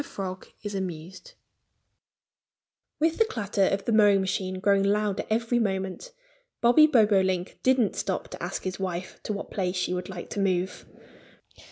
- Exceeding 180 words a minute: No, average, 155 wpm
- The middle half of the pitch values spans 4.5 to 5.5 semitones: No, average, 2.8 semitones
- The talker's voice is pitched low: No, high, 195 Hz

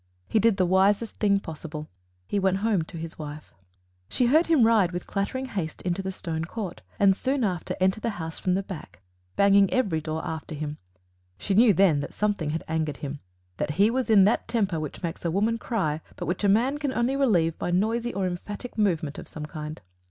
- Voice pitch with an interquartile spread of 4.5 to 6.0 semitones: Yes, average, 5.2 semitones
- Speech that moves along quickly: Yes, fast, 210 wpm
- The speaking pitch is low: No, high, 190 Hz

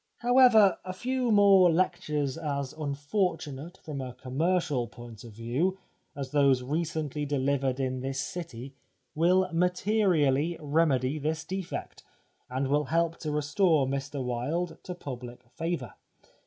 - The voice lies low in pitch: No, medium, 150 Hz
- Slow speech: Yes, slow, 130 wpm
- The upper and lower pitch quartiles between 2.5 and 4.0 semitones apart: No, average, 4.9 semitones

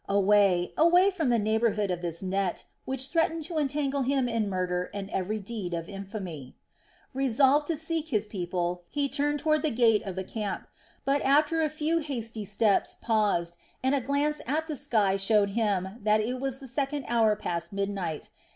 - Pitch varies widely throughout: Yes, wide, 6.4 semitones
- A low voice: No, high, 225 Hz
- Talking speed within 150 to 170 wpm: No, average, 180 wpm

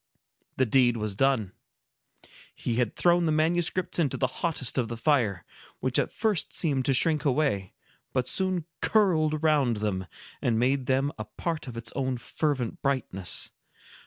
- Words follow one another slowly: No, average, 160 wpm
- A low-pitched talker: Yes, low, 130 Hz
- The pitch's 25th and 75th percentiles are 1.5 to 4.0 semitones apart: No, average, 5.0 semitones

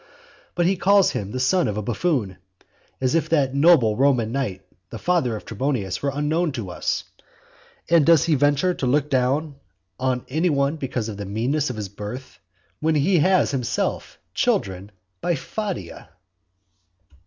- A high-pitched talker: No, low, 135 Hz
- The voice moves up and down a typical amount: No, wide, 6.0 semitones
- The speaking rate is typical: Yes, average, 165 wpm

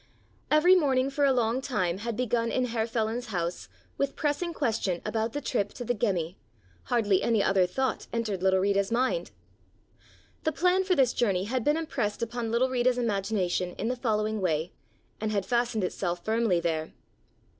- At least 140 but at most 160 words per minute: No, average, 175 wpm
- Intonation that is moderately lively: Yes, average, 4.5 semitones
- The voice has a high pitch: Yes, high, 230 Hz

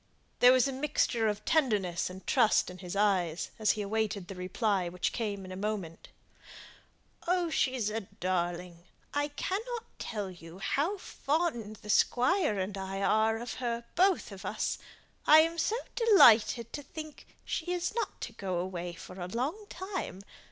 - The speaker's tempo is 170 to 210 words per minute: No, average, 160 wpm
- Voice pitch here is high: Yes, high, 215 Hz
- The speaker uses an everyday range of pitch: No, wide, 7.6 semitones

